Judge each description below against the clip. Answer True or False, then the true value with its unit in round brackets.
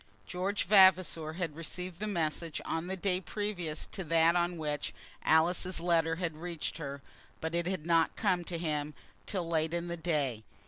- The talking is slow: False (175 wpm)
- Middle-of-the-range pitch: True (170 Hz)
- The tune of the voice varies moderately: False (2.2 semitones)